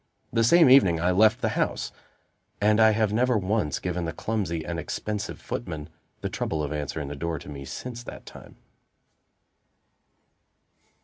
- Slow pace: No, average, 160 wpm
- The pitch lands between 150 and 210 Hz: No, very low, 95 Hz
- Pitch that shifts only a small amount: No, wide, 5.6 semitones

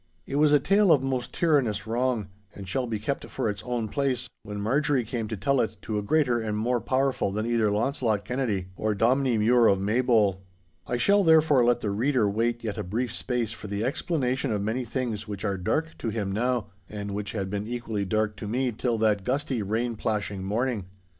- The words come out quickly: Yes, fast, 210 wpm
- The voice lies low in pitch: Yes, low, 115 Hz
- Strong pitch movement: No, average, 3.6 semitones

